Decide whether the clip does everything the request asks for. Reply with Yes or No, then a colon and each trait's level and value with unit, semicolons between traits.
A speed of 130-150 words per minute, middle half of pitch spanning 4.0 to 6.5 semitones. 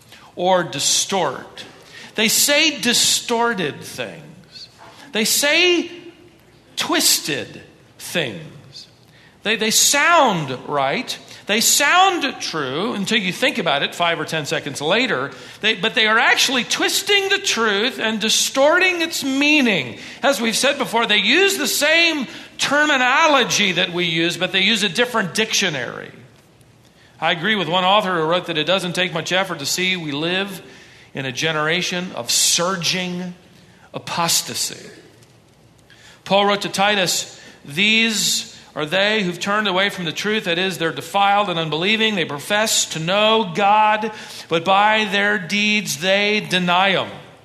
Yes: average, 140 wpm; average, 4.9 semitones